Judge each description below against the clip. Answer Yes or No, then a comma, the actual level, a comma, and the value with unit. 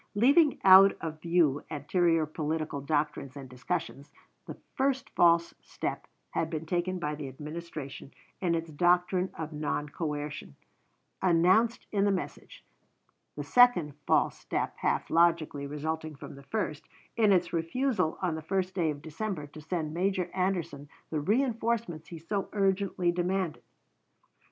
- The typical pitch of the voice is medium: Yes, medium, 170 Hz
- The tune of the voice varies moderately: Yes, average, 3.8 semitones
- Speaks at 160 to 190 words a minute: No, average, 140 wpm